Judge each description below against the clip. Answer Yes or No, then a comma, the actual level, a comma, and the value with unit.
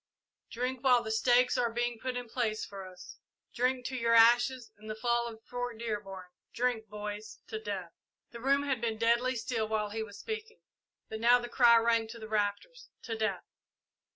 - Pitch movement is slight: Yes, narrow, 2.2 semitones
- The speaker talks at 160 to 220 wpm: Yes, average, 190 wpm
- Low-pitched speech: No, high, 230 Hz